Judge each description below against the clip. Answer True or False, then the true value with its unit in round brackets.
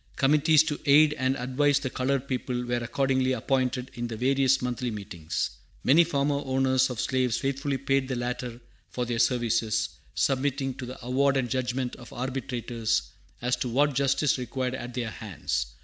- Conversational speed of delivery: True (165 wpm)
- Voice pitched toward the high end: False (130 Hz)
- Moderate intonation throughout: False (1.9 semitones)